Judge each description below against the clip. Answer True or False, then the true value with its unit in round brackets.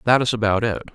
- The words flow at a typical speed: False (255 wpm)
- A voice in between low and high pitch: False (115 Hz)